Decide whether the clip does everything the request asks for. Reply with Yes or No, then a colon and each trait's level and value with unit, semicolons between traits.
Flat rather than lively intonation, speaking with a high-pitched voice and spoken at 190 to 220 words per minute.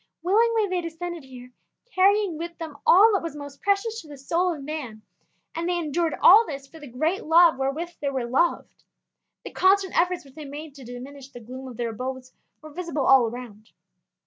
No: average, 4.9 semitones; very high, 310 Hz; average, 200 wpm